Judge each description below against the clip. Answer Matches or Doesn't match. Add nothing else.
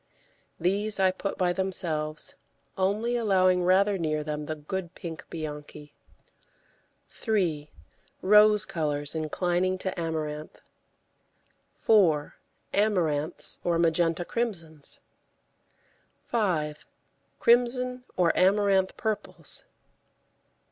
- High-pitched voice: Doesn't match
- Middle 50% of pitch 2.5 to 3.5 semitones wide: Doesn't match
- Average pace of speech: Doesn't match